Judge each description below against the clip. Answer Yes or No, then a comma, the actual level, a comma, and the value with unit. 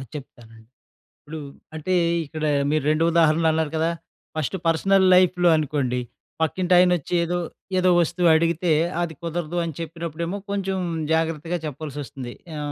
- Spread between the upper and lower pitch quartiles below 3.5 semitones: Yes, narrow, 2.4 semitones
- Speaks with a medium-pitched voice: Yes, medium, 165 Hz